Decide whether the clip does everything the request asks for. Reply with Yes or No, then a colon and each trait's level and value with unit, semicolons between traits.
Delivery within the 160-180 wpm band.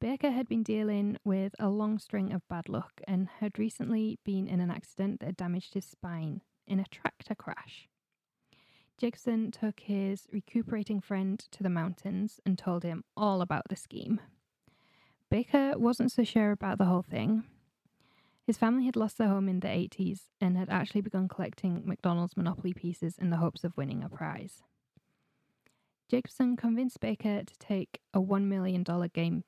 Yes: average, 165 wpm